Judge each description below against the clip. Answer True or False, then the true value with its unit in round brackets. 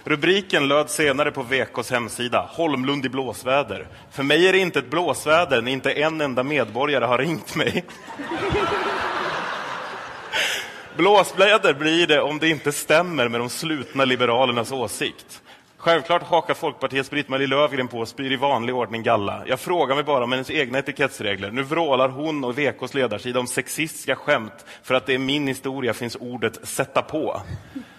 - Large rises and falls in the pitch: False (3.2 semitones)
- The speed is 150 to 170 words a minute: True (160 wpm)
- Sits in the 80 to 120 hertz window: False (135 Hz)